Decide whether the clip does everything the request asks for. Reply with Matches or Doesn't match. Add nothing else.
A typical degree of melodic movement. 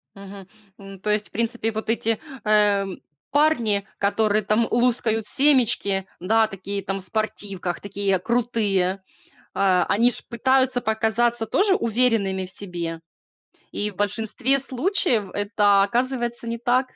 Matches